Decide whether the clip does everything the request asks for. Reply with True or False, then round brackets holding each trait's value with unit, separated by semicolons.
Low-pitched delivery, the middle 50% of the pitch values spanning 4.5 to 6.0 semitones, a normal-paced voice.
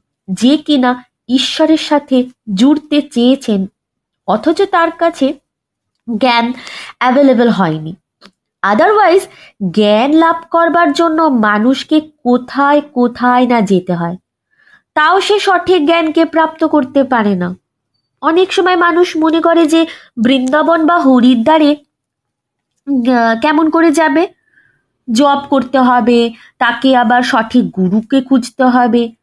False (270 Hz; 5.3 semitones; 105 wpm)